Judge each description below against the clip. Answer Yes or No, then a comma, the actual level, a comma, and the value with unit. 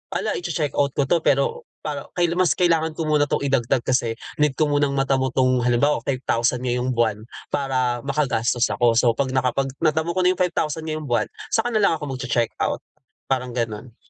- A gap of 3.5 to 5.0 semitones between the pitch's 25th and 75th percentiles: Yes, average, 4.2 semitones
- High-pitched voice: No, low, 135 Hz